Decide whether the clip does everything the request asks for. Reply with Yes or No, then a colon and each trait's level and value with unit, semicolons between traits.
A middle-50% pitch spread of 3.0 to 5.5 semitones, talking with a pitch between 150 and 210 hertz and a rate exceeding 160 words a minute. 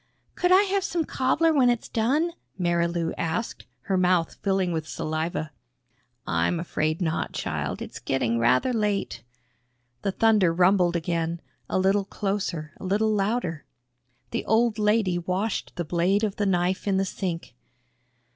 No: average, 4.4 semitones; medium, 185 Hz; average, 145 wpm